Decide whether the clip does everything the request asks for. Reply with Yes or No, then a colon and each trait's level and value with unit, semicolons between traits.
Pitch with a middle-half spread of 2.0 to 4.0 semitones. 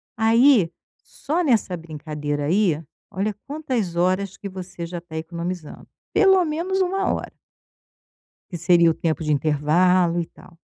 No: wide, 5.4 semitones